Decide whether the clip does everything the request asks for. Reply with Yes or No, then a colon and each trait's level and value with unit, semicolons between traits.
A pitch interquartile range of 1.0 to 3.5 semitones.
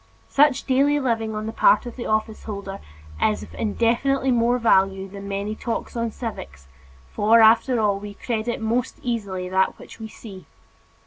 Yes: average, 3.0 semitones